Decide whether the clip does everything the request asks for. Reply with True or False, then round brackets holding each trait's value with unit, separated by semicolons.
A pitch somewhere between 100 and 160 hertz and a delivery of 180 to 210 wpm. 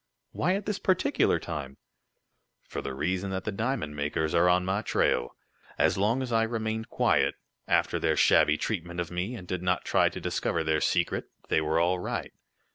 False (90 Hz; 190 wpm)